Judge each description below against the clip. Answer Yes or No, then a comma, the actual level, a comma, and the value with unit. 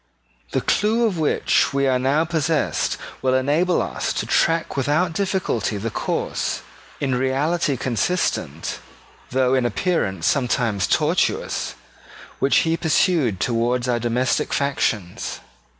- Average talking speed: No, slow, 120 wpm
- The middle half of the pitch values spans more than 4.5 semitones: Yes, average, 5.2 semitones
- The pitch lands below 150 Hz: Yes, low, 135 Hz